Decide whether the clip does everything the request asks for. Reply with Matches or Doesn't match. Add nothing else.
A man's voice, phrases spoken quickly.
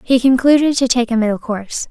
Doesn't match